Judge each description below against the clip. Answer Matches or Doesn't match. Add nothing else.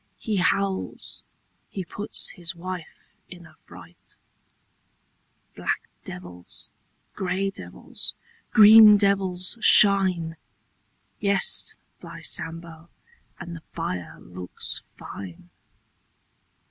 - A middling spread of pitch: Matches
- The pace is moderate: Doesn't match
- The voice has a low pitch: Doesn't match